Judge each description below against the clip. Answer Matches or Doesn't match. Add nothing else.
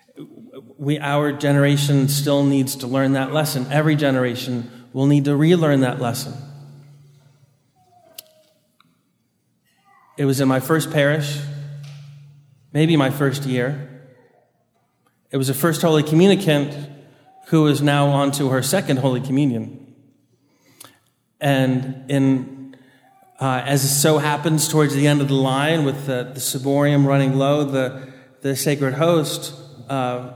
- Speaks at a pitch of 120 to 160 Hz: Matches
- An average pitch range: Doesn't match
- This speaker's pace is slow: Matches